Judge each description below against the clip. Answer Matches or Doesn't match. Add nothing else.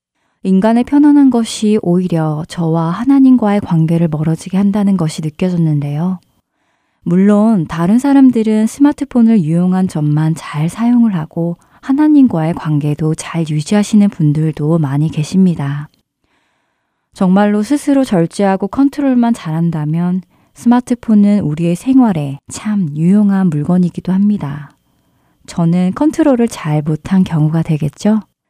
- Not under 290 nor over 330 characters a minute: Matches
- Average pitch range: Doesn't match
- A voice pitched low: Doesn't match